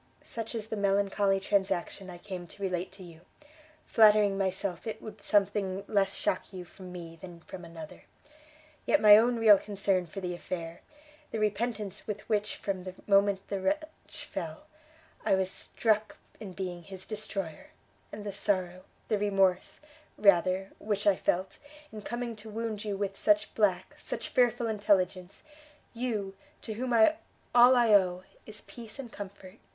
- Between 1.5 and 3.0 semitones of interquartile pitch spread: Yes, narrow, 2.4 semitones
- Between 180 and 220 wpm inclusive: No, average, 160 wpm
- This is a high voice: Yes, high, 200 Hz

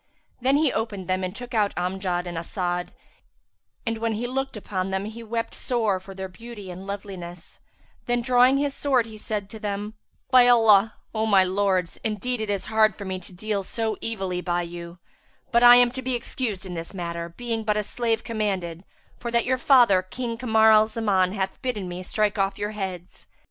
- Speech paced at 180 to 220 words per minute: Yes, average, 200 wpm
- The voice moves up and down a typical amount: Yes, average, 3.8 semitones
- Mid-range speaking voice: No, high, 210 Hz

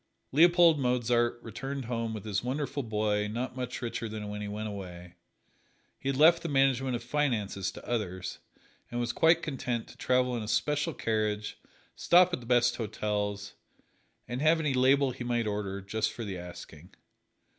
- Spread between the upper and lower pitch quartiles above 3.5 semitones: Yes, average, 4.3 semitones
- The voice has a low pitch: Yes, low, 120 Hz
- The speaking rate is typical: Yes, average, 175 wpm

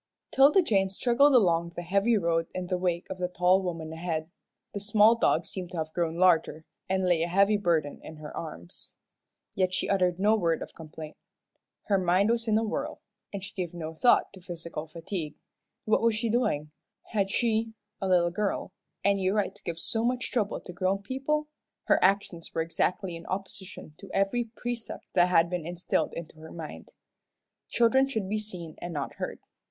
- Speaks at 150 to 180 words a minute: No, average, 190 wpm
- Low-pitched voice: No, medium, 185 Hz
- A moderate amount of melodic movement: Yes, average, 4.1 semitones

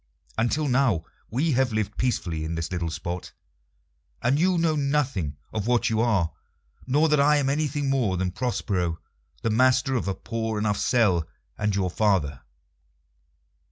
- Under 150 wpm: No, average, 155 wpm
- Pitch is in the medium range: No, low, 115 Hz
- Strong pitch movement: Yes, wide, 6.6 semitones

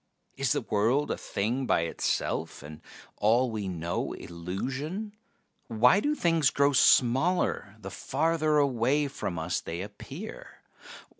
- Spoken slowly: Yes, slow, 130 wpm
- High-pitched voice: No, low, 125 Hz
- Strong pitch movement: Yes, wide, 7.3 semitones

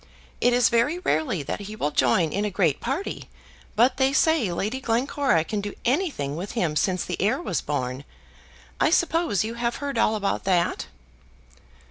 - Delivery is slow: No, average, 175 wpm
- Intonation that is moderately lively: No, wide, 7.3 semitones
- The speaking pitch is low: No, high, 215 Hz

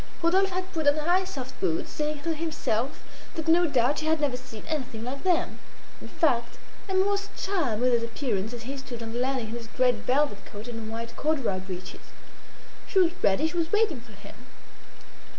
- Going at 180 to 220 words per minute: Yes, average, 200 wpm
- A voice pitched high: Yes, very high, 265 Hz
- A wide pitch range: Yes, wide, 5.8 semitones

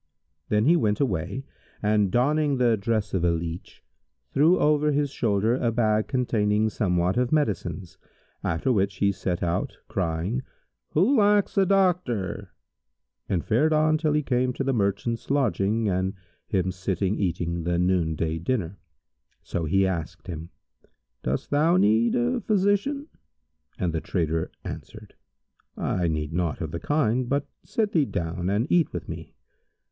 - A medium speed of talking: Yes, average, 155 wpm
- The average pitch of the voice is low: Yes, low, 105 Hz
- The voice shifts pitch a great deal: Yes, wide, 8.0 semitones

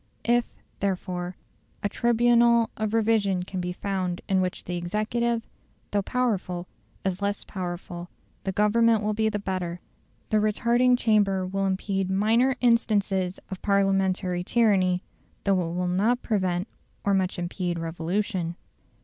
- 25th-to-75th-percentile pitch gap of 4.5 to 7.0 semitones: No, average, 3.2 semitones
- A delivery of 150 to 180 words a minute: No, slow, 135 wpm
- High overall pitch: Yes, high, 195 Hz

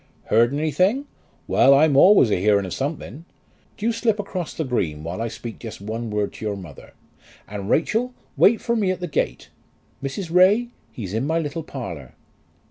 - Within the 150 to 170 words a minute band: No, average, 185 wpm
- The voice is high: No, medium, 140 Hz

